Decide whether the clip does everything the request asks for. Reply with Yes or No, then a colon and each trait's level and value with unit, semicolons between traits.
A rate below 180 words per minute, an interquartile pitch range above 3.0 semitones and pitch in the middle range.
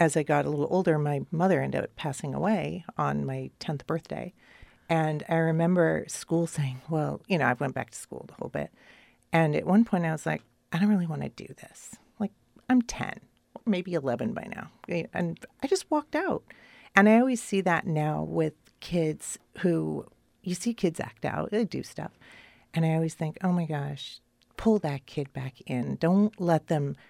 No: average, 200 wpm; average, 4.7 semitones; medium, 165 Hz